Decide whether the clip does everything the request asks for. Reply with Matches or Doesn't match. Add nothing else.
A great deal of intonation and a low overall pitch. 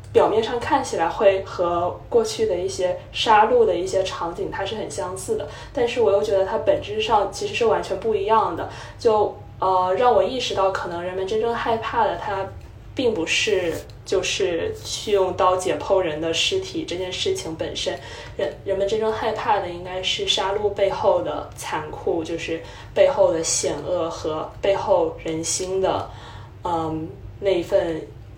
Doesn't match